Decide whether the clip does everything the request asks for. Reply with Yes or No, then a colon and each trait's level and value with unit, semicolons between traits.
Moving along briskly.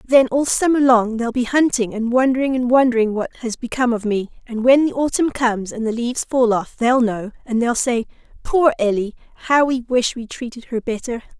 Yes: fast, 210 wpm